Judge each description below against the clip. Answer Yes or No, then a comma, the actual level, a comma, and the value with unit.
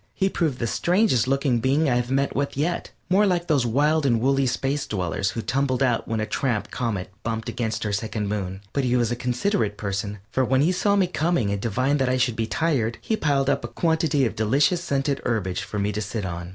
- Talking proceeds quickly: Yes, fast, 230 wpm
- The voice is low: Yes, low, 125 Hz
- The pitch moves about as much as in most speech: Yes, average, 4.7 semitones